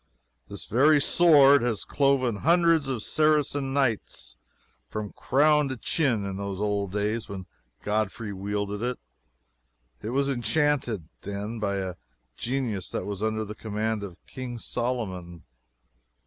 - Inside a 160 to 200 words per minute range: No, slow, 135 wpm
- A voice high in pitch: No, low, 110 Hz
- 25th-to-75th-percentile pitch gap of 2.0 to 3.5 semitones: No, average, 5.1 semitones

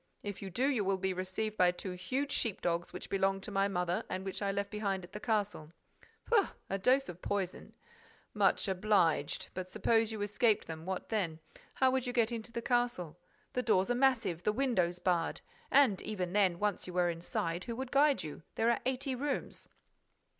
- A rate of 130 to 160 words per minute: No, average, 200 wpm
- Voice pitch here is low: No, high, 200 Hz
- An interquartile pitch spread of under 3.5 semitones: No, average, 4.6 semitones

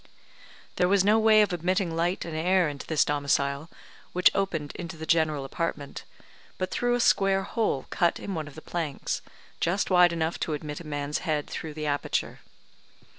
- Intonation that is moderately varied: Yes, average, 3.8 semitones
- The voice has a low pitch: No, medium, 165 Hz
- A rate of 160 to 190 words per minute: Yes, average, 180 wpm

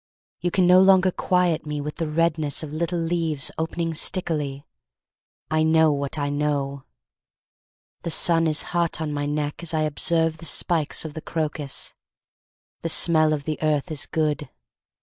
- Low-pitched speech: No, medium, 155 Hz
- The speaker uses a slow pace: No, average, 165 wpm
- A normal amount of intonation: No, narrow, 2.0 semitones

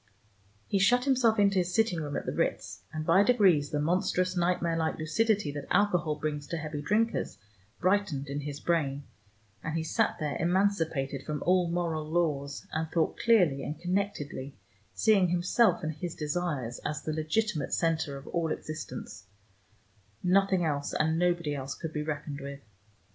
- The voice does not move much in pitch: No, average, 3.7 semitones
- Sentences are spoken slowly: No, average, 165 wpm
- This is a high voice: No, medium, 165 Hz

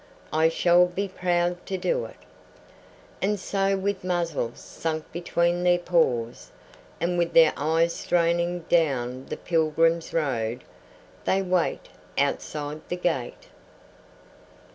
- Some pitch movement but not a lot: No, narrow, 2.2 semitones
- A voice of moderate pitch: Yes, medium, 170 Hz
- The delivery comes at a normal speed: No, slow, 120 wpm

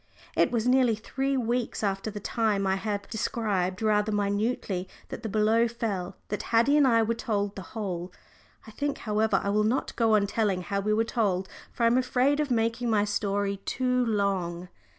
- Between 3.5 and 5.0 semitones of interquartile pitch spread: No, average, 2.7 semitones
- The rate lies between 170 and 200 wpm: Yes, average, 190 wpm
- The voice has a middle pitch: No, high, 215 Hz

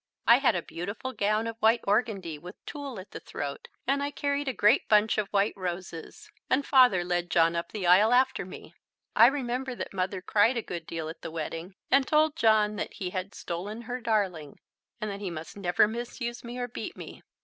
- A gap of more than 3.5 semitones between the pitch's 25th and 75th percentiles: Yes, average, 5.3 semitones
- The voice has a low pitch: No, high, 210 Hz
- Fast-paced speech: Yes, fast, 210 wpm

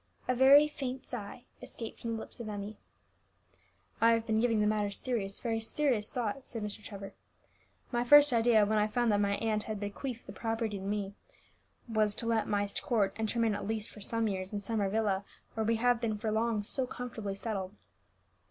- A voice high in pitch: Yes, high, 220 Hz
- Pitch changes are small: Yes, narrow, 2.2 semitones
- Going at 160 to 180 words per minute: No, fast, 205 wpm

